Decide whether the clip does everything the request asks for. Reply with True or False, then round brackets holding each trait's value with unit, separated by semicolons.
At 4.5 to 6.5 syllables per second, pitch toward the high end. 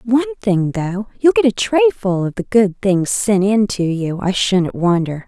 False (4.3 syllables/s; 205 Hz)